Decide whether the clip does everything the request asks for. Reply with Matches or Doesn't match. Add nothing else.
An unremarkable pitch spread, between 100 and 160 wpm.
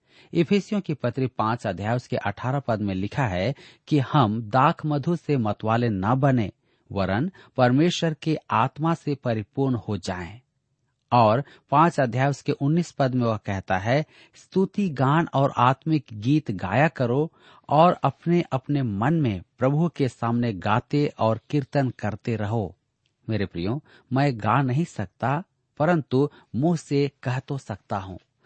Matches